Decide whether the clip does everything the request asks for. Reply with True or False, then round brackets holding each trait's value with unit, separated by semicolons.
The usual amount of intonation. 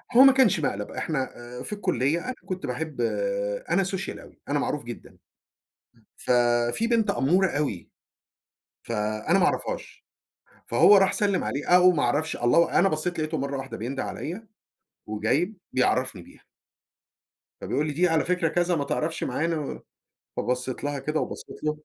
False (5.9 semitones)